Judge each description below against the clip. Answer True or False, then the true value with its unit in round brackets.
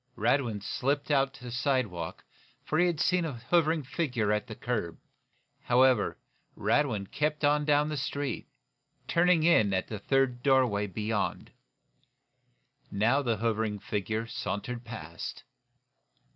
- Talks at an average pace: False (130 wpm)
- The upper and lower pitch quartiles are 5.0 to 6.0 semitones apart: True (5.3 semitones)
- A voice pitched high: False (125 Hz)